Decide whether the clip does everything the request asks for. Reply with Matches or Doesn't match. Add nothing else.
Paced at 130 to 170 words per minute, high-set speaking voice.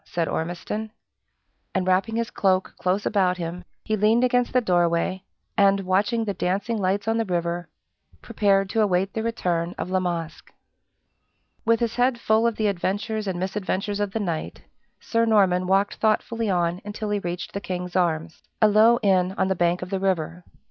Doesn't match